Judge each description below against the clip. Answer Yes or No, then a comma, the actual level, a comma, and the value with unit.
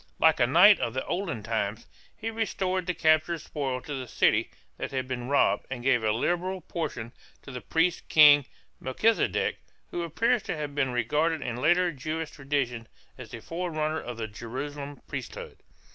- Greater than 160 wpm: Yes, average, 170 wpm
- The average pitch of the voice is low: No, medium, 145 Hz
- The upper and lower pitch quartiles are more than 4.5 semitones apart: Yes, average, 5.2 semitones